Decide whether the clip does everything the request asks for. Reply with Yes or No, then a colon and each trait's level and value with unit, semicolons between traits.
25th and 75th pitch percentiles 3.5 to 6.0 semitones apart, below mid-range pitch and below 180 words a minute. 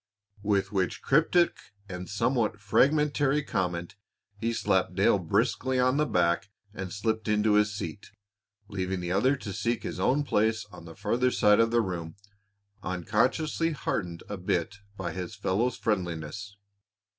Yes: average, 4.8 semitones; low, 105 Hz; average, 145 wpm